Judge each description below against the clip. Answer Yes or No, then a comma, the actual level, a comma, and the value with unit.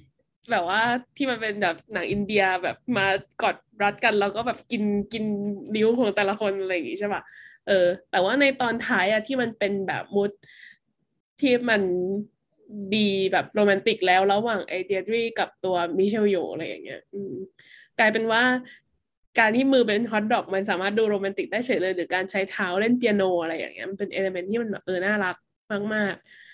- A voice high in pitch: Yes, high, 205 Hz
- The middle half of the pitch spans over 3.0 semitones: No, average, 2.7 semitones